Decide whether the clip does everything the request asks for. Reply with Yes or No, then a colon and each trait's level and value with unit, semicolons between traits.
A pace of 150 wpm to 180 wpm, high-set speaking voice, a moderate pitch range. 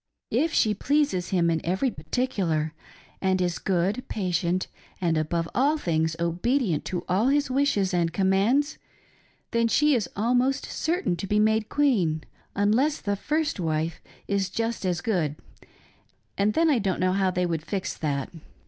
No: average, 160 wpm; high, 195 Hz; wide, 6.3 semitones